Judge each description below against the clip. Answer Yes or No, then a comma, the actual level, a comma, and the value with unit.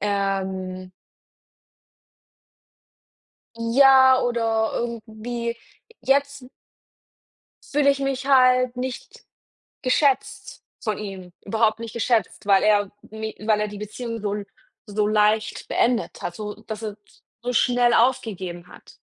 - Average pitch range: Yes, average, 3.3 semitones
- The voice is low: No, high, 225 Hz